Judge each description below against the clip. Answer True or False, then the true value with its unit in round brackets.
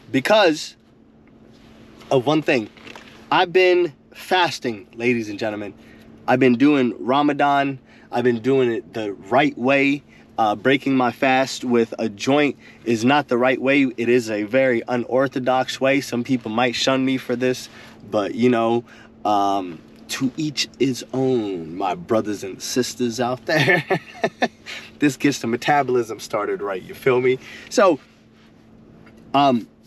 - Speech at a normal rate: True (145 wpm)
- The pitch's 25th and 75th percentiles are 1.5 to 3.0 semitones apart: True (2.5 semitones)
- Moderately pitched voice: False (125 Hz)